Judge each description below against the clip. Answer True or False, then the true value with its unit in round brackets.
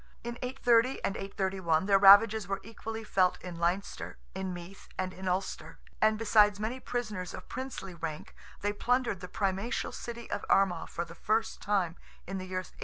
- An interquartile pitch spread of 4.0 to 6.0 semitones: False (3.4 semitones)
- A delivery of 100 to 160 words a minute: False (180 wpm)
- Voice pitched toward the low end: False (195 Hz)